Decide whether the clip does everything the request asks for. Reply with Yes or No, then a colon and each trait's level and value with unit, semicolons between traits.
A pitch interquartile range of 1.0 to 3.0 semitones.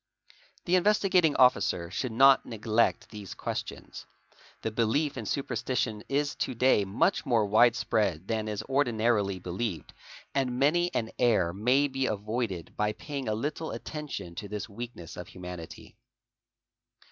No: average, 4.7 semitones